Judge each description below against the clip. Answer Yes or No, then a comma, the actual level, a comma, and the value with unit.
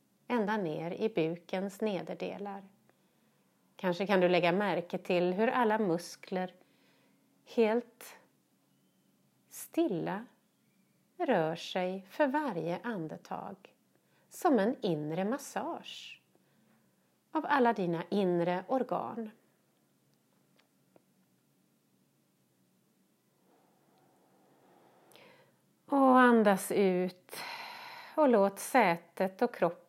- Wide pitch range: Yes, wide, 5.7 semitones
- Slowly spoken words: Yes, slow, 75 wpm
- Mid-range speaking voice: No, high, 200 Hz